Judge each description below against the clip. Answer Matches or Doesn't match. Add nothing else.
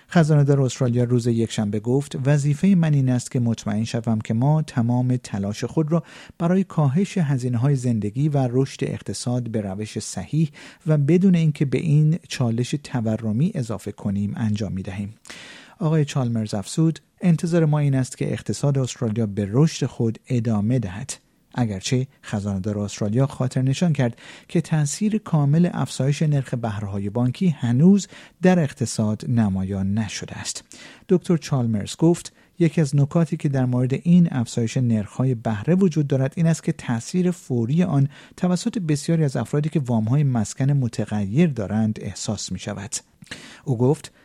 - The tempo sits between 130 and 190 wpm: Matches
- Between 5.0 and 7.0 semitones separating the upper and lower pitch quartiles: Matches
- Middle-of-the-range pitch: Doesn't match